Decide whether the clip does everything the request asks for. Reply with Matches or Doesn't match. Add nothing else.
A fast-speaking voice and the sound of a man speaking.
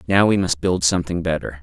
Matches